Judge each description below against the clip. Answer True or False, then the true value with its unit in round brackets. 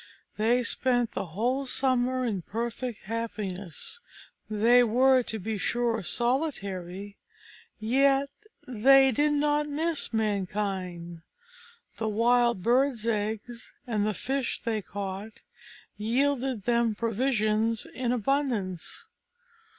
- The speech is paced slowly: True (105 wpm)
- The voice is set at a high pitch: True (230 Hz)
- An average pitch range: True (3.6 semitones)